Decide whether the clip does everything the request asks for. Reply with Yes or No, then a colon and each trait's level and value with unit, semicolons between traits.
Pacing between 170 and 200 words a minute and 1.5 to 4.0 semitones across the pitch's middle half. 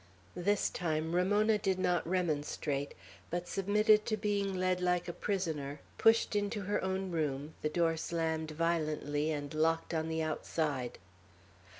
No: average, 140 wpm; average, 3.7 semitones